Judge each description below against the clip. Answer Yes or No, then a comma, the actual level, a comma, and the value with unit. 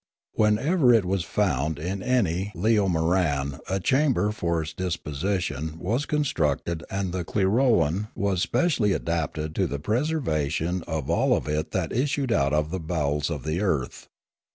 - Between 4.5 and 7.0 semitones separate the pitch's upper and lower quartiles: Yes, wide, 5.4 semitones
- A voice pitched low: Yes, very low, 90 Hz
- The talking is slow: No, average, 150 wpm